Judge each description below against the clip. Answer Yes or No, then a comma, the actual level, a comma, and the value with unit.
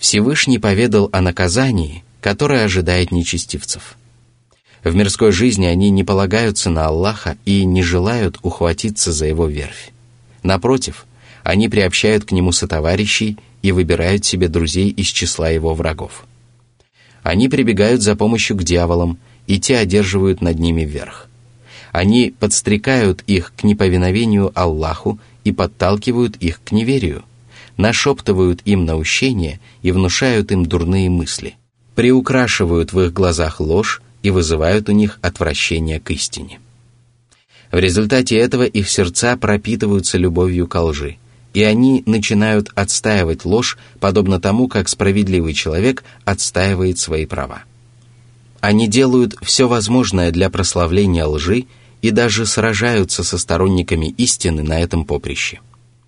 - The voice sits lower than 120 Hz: Yes, low, 100 Hz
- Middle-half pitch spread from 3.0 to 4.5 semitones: No, average, 5.0 semitones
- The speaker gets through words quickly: No, average, 125 wpm